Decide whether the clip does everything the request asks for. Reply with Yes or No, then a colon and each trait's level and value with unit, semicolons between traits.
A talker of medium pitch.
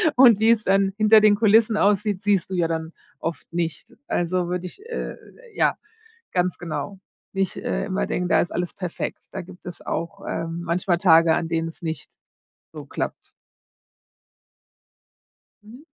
Yes: medium, 180 Hz